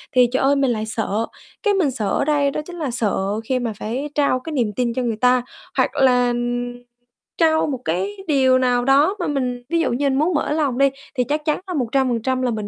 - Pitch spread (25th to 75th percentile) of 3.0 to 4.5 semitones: Yes, average, 3.3 semitones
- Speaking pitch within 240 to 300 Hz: Yes, very high, 260 Hz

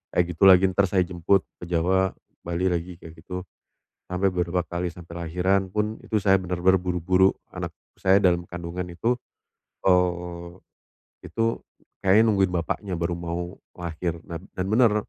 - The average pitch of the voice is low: Yes, very low, 90 Hz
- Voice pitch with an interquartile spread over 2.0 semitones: No, narrow, 1.7 semitones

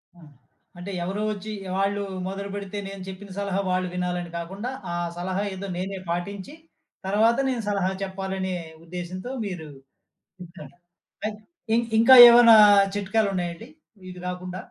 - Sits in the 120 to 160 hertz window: No, high, 190 Hz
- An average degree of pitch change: No, narrow, 2.0 semitones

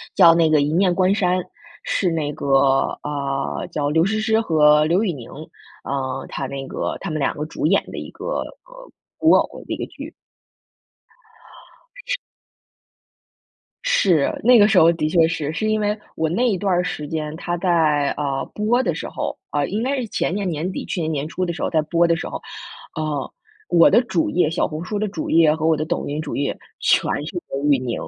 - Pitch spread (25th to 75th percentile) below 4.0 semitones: No, average, 4.4 semitones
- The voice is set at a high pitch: No, medium, 165 Hz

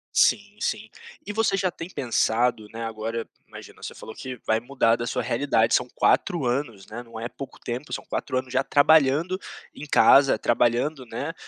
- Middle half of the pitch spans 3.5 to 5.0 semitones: Yes, average, 3.9 semitones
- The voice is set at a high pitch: No, low, 125 Hz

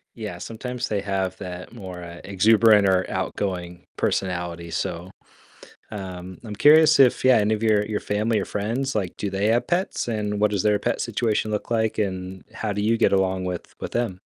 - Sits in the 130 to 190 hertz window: No, low, 105 Hz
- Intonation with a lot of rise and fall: No, average, 3.2 semitones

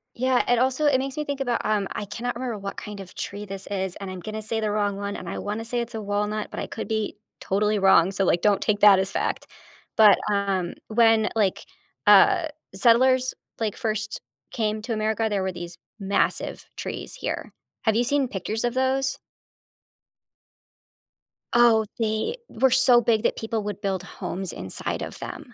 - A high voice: Yes, high, 215 Hz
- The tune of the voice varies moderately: Yes, average, 3.1 semitones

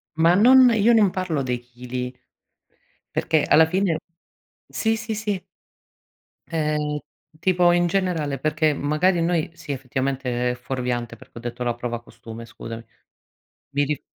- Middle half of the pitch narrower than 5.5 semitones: No, wide, 6.2 semitones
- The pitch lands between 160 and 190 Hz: No, medium, 150 Hz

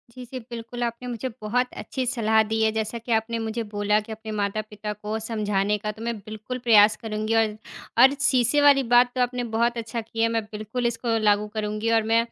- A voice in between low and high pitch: No, high, 225 Hz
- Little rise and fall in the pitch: Yes, narrow, 2.1 semitones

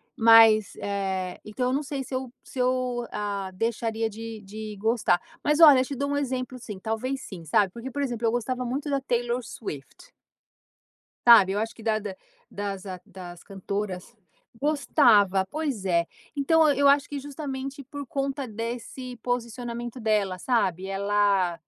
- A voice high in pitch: Yes, high, 230 Hz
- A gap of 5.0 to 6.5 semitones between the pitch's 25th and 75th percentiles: No, average, 4.5 semitones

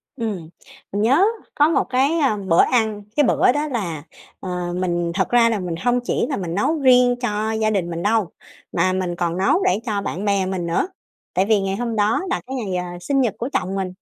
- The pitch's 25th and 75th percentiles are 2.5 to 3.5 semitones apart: No, average, 5.1 semitones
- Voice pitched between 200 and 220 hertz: Yes, high, 205 Hz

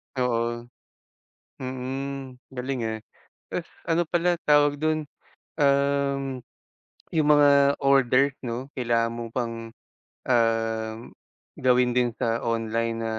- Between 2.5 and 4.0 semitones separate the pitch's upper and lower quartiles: Yes, average, 3.2 semitones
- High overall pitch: No, low, 125 Hz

